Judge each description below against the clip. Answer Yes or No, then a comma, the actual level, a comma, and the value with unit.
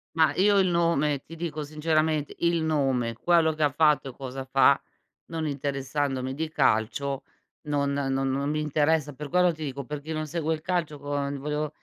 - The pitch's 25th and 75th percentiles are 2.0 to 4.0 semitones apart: Yes, narrow, 2.4 semitones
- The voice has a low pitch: No, medium, 150 Hz